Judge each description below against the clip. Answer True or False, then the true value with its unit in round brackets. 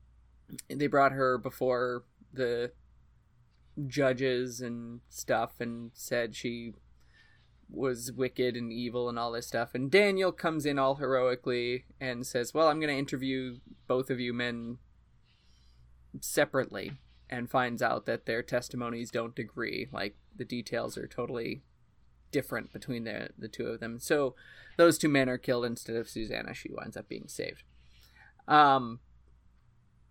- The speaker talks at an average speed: True (145 wpm)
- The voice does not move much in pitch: True (2.2 semitones)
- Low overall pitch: True (120 Hz)